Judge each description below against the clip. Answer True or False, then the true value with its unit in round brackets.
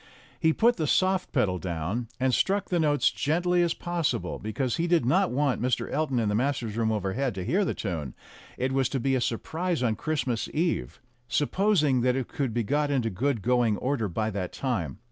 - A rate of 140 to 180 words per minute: False (205 wpm)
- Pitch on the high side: False (130 Hz)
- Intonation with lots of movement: True (6.0 semitones)